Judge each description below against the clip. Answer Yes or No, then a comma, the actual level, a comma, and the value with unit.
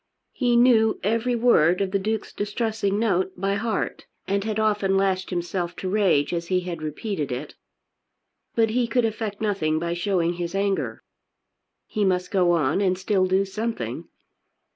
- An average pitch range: Yes, average, 3.4 semitones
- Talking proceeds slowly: No, average, 165 wpm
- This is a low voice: No, high, 195 Hz